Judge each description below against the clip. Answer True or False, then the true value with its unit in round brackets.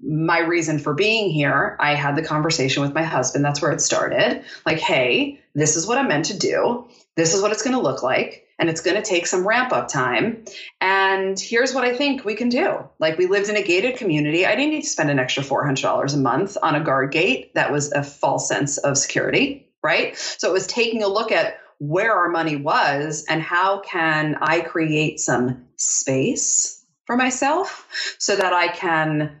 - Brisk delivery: True (210 wpm)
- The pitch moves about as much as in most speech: False (6.1 semitones)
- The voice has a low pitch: False (175 Hz)